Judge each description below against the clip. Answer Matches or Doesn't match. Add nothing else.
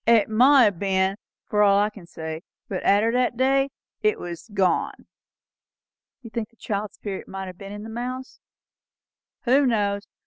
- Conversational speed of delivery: Matches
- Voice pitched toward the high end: Matches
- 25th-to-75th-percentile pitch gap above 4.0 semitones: Doesn't match